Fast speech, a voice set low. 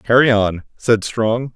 No: average, 155 wpm; low, 115 Hz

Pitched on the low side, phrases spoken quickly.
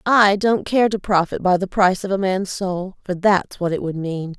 No: high, 190 Hz; fast, 230 wpm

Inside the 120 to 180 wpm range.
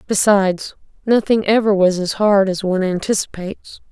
Yes: average, 140 wpm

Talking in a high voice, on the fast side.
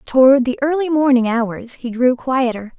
No: very high, 260 Hz; average, 170 wpm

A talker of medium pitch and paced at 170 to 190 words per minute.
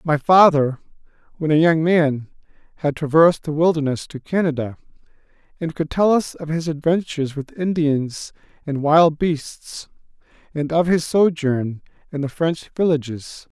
No: medium, 155 Hz; average, 140 wpm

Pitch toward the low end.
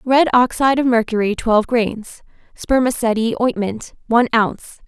No: high, 235 Hz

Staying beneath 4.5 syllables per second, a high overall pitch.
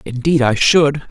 No: 4.3 syllables/s; medium, 140 Hz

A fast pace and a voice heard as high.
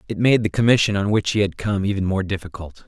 No: fast, 250 wpm; low, 100 Hz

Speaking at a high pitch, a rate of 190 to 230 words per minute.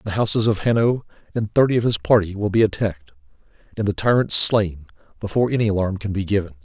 No: low, 100 Hz; average, 200 wpm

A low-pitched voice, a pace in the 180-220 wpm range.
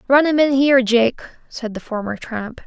No: high, 245 Hz; fast, 205 wpm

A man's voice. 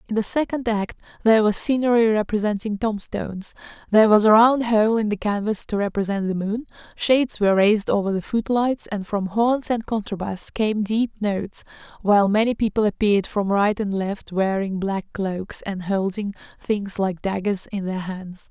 No: female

